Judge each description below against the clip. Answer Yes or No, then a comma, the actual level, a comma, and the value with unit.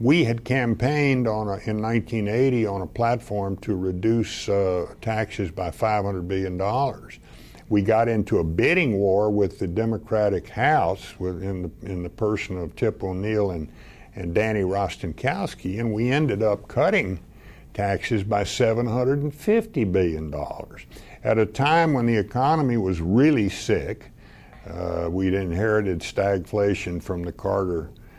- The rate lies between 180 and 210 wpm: No, slow, 135 wpm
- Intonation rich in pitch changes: No, average, 3.3 semitones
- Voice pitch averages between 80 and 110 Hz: Yes, low, 105 Hz